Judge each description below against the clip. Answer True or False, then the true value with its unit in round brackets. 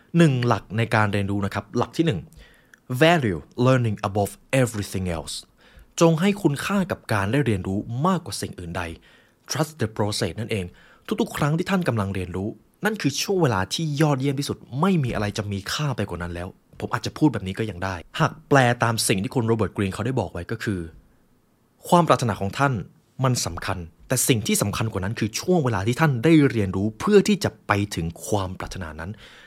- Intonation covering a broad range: True (6.6 semitones)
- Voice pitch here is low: True (115 Hz)